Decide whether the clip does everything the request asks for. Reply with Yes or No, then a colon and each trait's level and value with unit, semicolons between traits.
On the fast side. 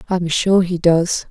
Yes: fast, 230 wpm